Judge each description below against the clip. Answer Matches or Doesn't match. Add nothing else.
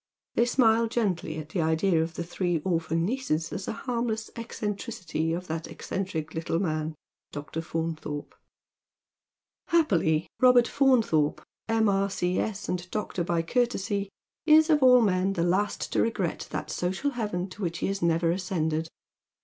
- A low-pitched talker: Doesn't match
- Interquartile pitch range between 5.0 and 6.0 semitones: Matches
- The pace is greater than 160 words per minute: Doesn't match